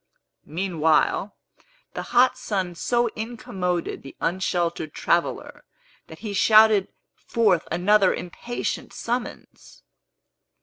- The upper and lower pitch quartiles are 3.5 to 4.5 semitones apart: Yes, average, 4.1 semitones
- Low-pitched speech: No, high, 190 Hz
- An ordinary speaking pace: No, slow, 90 wpm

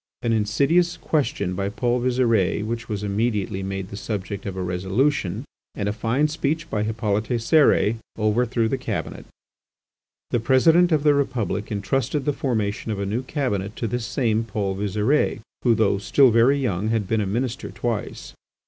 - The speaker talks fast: No, average, 165 wpm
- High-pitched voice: No, low, 115 Hz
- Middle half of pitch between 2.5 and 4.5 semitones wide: Yes, average, 4.1 semitones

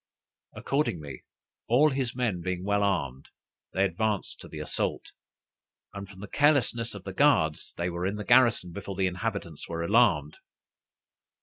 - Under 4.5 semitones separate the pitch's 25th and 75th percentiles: No, average, 5.0 semitones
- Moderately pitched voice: No, low, 100 Hz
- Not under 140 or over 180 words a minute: Yes, average, 150 wpm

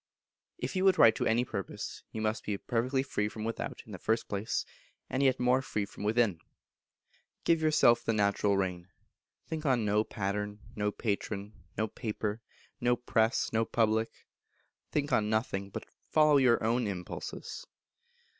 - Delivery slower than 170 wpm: Yes, average, 160 wpm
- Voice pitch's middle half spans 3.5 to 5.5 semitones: No, average, 3.1 semitones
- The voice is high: No, low, 110 Hz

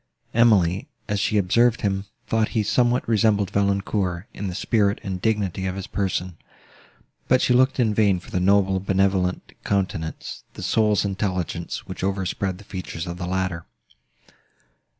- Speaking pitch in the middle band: No, low, 100 Hz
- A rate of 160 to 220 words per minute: No, average, 150 wpm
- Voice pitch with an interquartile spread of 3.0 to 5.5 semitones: No, narrow, 2.4 semitones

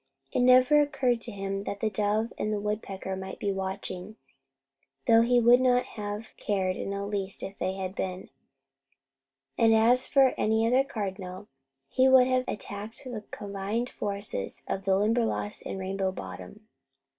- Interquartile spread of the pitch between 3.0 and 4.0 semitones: Yes, average, 3.4 semitones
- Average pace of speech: Yes, average, 160 wpm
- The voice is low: No, high, 210 Hz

